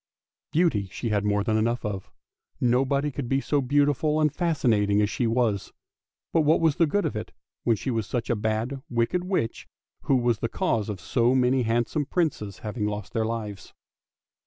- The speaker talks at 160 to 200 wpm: Yes, average, 185 wpm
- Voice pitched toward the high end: No, low, 120 Hz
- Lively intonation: No, average, 4.7 semitones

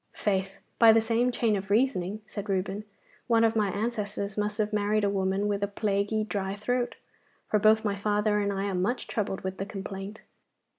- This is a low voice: No, high, 205 Hz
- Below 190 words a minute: No, average, 195 wpm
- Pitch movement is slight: Yes, narrow, 1.7 semitones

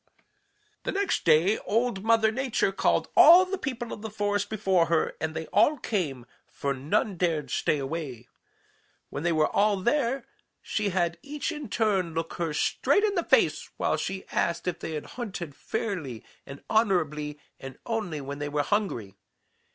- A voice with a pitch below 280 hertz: Yes, high, 190 Hz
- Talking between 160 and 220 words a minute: Yes, average, 170 wpm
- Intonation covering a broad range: Yes, wide, 6.4 semitones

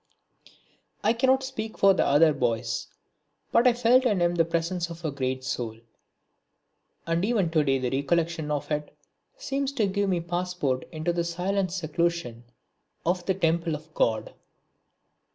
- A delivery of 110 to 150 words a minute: No, average, 160 wpm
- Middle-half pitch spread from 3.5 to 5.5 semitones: Yes, average, 4.6 semitones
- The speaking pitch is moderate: Yes, medium, 170 Hz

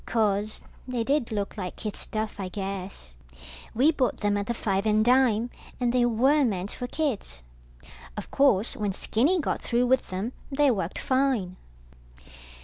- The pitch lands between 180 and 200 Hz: No, high, 225 Hz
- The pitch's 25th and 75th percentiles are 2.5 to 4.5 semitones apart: Yes, average, 4.2 semitones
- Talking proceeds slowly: No, average, 160 wpm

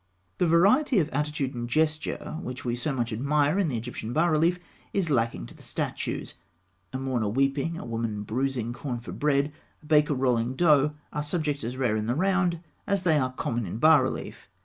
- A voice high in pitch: No, medium, 140 Hz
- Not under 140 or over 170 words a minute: No, average, 195 wpm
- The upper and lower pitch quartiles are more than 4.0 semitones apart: Yes, average, 4.6 semitones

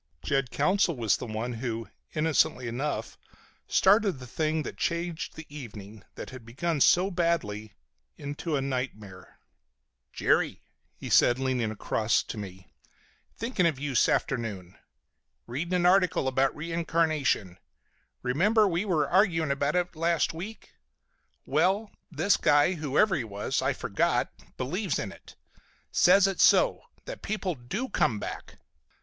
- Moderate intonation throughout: No, wide, 6.5 semitones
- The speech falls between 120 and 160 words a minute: Yes, slow, 135 wpm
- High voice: No, medium, 150 Hz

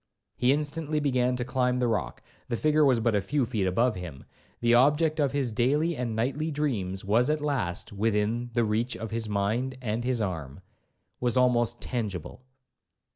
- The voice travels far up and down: No, average, 4.0 semitones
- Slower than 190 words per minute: Yes, average, 165 wpm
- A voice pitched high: No, low, 120 Hz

